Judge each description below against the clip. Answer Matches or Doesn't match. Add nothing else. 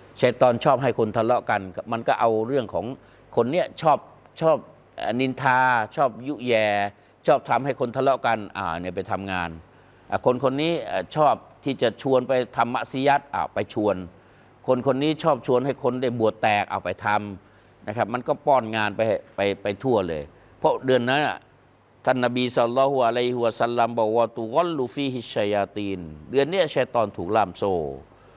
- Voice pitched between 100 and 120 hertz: Matches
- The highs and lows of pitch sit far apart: Doesn't match